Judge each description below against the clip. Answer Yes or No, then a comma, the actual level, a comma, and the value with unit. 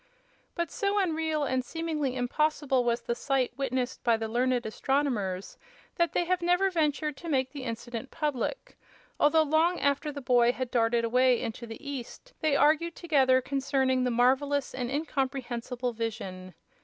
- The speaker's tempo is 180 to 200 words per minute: No, average, 155 wpm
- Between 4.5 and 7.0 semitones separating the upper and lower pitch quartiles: No, average, 3.8 semitones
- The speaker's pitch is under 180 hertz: No, very high, 265 Hz